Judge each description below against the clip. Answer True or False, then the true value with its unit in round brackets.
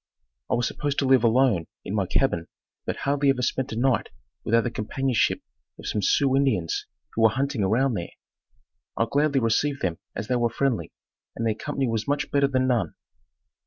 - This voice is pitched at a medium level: False (125 Hz)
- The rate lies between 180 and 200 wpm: True (190 wpm)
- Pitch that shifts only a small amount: False (3.7 semitones)